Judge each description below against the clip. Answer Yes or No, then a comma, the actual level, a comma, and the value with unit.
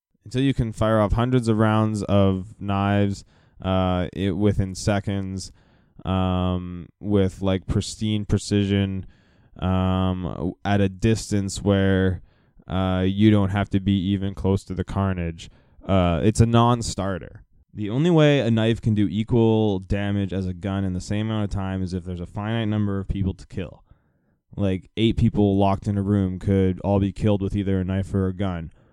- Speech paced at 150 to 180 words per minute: Yes, average, 175 wpm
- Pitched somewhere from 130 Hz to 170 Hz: No, low, 100 Hz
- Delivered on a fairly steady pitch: Yes, narrow, 2.0 semitones